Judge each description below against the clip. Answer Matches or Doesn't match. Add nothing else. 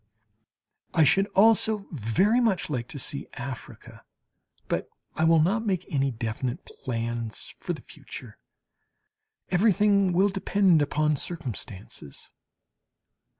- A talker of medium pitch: Matches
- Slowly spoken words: Matches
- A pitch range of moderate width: Doesn't match